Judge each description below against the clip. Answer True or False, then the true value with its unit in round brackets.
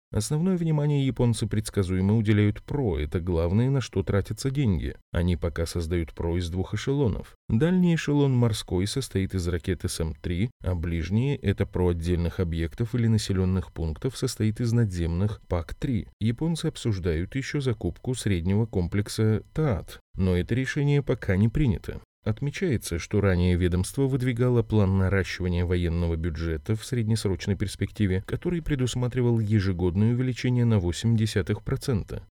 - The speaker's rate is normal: True (130 wpm)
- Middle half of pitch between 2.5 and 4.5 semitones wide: False (5.4 semitones)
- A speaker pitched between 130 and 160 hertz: False (105 Hz)